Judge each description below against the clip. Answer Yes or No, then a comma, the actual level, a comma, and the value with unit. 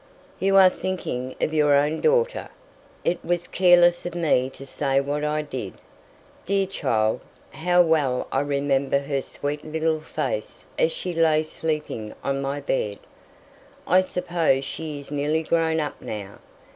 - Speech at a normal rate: Yes, average, 150 wpm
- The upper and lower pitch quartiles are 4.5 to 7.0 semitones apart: No, average, 3.9 semitones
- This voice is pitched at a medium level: Yes, medium, 155 Hz